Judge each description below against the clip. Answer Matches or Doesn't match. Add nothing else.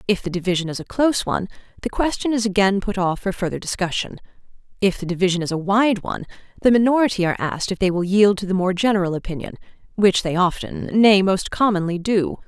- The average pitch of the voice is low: Doesn't match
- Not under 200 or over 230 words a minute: Matches